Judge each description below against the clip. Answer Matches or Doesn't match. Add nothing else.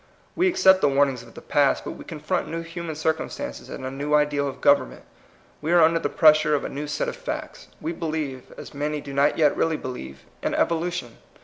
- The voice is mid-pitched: Matches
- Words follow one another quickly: Matches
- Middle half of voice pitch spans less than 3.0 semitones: Matches